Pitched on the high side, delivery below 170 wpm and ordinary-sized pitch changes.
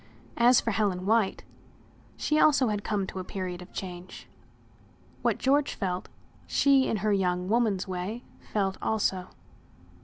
Yes: high, 200 Hz; average, 145 wpm; average, 3.9 semitones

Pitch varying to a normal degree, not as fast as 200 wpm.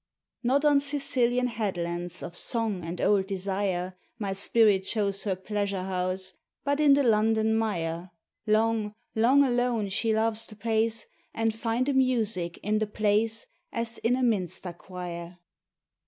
Yes: average, 3.4 semitones; average, 145 wpm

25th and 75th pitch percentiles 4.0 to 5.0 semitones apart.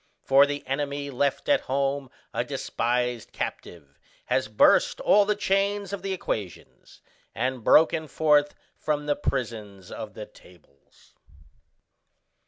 Yes: average, 4.6 semitones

